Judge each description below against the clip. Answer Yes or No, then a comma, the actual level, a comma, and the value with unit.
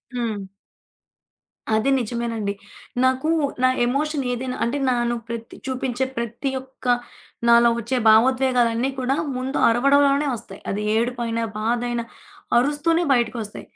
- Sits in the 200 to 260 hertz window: Yes, high, 245 Hz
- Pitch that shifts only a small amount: Yes, narrow, 2.2 semitones